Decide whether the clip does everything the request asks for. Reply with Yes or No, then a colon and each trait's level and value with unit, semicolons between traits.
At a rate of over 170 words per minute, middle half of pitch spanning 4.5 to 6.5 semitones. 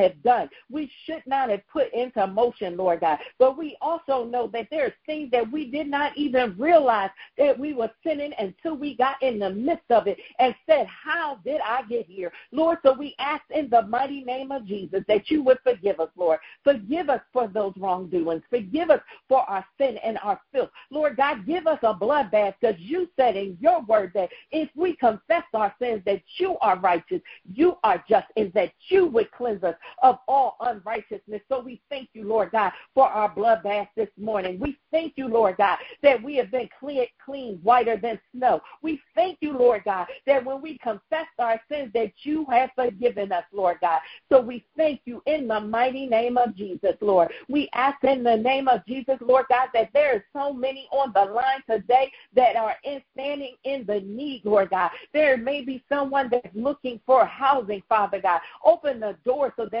Yes: fast, 205 wpm; average, 4.8 semitones